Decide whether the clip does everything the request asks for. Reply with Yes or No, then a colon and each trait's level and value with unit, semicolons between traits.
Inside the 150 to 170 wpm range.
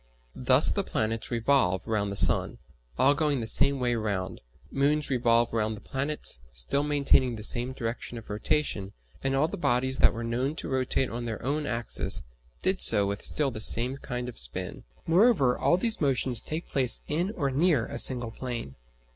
No: average, 185 wpm